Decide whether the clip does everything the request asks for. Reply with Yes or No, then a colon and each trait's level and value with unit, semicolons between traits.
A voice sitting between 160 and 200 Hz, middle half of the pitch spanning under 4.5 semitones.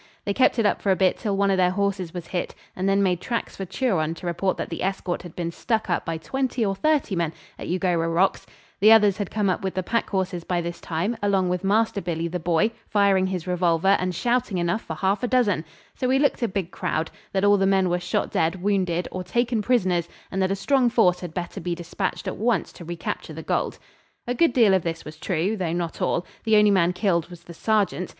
Yes: high, 190 Hz; average, 3.1 semitones